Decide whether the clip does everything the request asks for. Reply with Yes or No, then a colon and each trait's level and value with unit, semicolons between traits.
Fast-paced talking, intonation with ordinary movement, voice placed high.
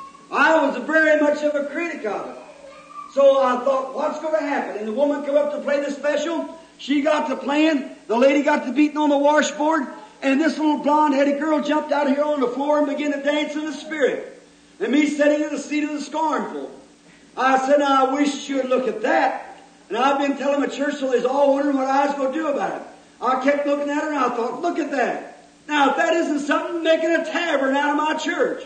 No: fast, 245 wpm; narrow, 1.8 semitones; very high, 290 Hz